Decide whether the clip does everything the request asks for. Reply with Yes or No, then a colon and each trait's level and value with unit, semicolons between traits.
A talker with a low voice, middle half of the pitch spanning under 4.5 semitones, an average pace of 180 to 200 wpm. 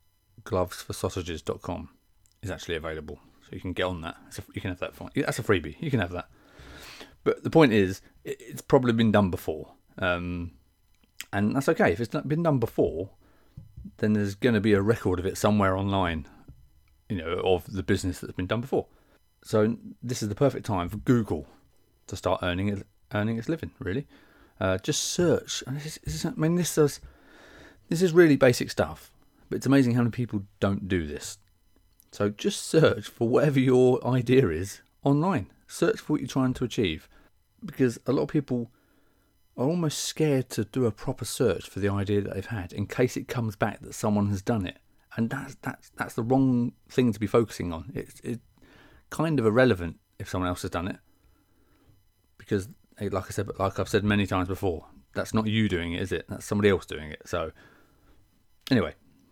No: low, 105 Hz; average, 5.1 semitones; average, 190 wpm